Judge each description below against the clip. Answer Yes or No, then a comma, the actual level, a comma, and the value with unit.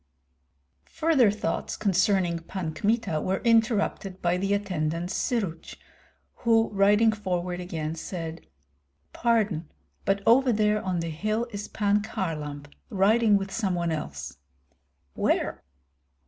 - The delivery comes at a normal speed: No, slow, 120 wpm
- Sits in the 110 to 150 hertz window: No, high, 195 Hz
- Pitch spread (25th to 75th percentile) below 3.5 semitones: No, average, 4.0 semitones